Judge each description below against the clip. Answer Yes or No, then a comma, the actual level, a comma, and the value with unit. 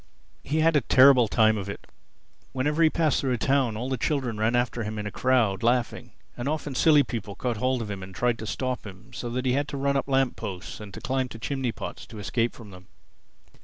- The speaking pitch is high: No, low, 125 Hz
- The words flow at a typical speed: No, fast, 240 wpm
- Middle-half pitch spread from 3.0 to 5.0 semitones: Yes, average, 3.6 semitones